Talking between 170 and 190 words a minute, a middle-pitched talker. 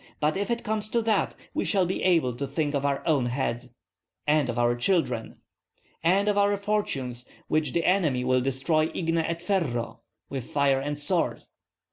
Yes: average, 180 wpm; medium, 150 Hz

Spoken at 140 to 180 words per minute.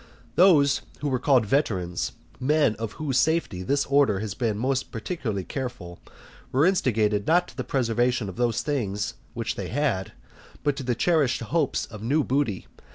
Yes: average, 160 wpm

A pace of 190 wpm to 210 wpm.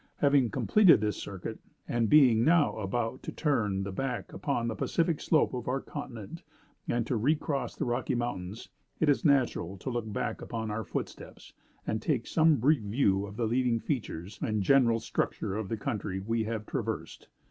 No: average, 180 wpm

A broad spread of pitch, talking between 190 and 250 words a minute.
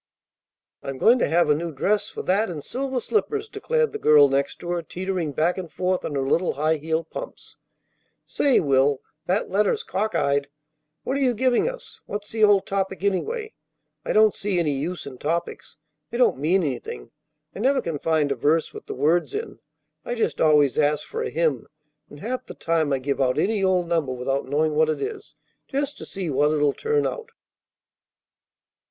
Yes: wide, 6.9 semitones; average, 195 wpm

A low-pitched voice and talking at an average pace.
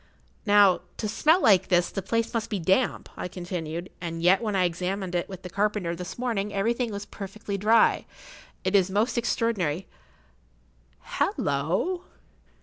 No: high, 195 Hz; average, 145 wpm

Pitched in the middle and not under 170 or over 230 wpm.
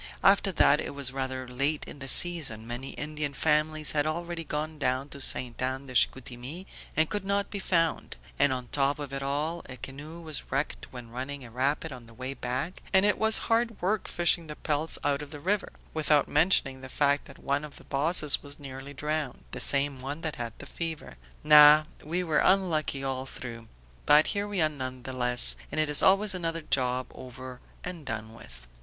Yes: medium, 145 Hz; fast, 205 wpm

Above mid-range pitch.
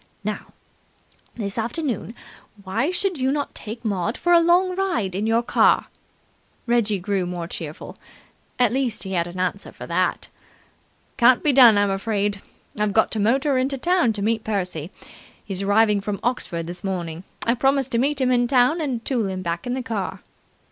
Yes: high, 225 Hz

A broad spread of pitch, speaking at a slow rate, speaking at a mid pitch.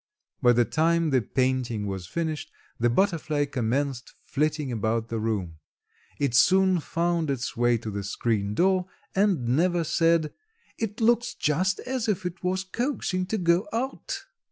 No: wide, 7.4 semitones; average, 155 wpm; medium, 155 Hz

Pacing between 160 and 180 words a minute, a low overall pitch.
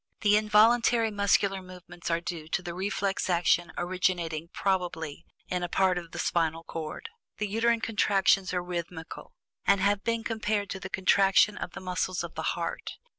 No: average, 170 wpm; medium, 185 Hz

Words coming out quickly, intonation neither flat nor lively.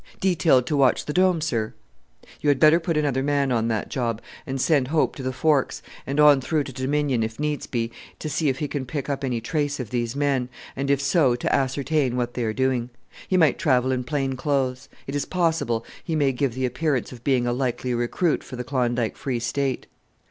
Yes: fast, 220 wpm; average, 3.0 semitones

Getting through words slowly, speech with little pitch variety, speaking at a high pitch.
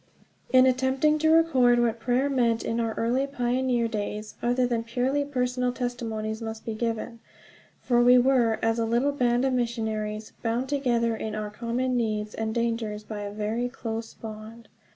No: average, 170 wpm; narrow, 2.2 semitones; high, 235 Hz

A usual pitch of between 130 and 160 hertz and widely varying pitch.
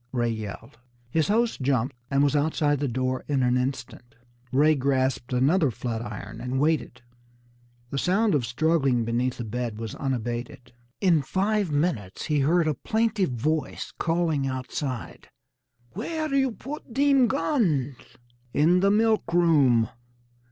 Yes: medium, 140 Hz; wide, 6.0 semitones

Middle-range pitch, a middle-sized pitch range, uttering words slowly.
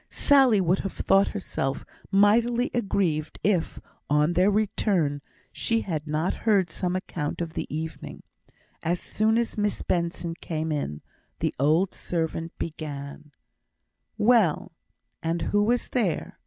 Yes: medium, 180 Hz; average, 4.9 semitones; slow, 130 wpm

